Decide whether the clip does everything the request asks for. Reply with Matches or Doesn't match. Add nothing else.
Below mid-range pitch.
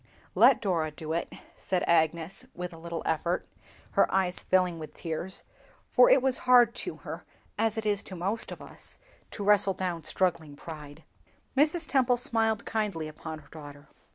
Doesn't match